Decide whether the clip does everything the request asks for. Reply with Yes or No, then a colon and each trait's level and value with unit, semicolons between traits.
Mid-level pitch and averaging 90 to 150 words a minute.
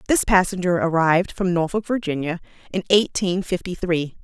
Yes: medium, 180 Hz; average, 140 wpm